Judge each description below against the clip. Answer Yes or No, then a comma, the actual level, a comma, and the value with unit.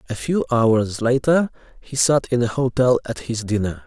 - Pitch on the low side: Yes, low, 120 Hz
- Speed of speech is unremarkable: Yes, average, 185 wpm